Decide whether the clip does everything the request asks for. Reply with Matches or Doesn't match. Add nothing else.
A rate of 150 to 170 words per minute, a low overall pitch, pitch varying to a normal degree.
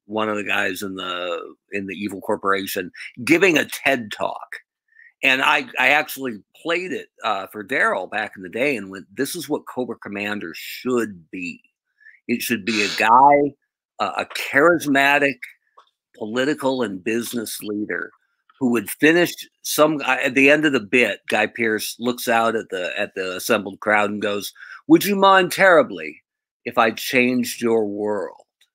Doesn't match